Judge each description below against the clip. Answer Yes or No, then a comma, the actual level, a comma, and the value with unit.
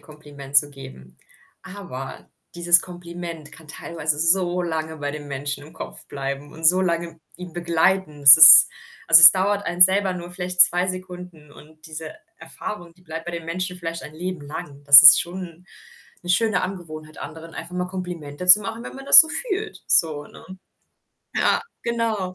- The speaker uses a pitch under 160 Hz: No, medium, 170 Hz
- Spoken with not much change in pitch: No, average, 3.0 semitones